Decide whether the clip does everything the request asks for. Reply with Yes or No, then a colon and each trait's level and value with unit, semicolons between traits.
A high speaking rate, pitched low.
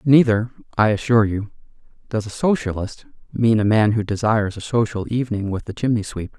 No: average, 180 wpm; low, 110 Hz